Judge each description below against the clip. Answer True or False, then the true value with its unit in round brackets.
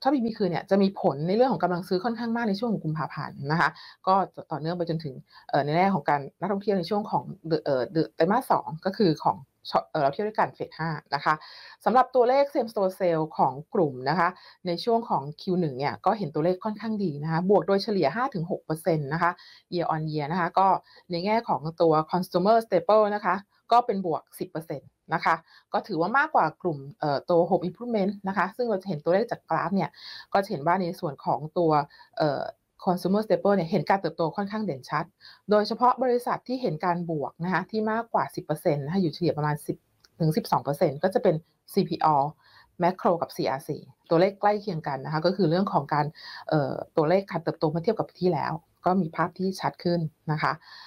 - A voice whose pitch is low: False (175 Hz)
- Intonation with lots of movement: False (3.8 semitones)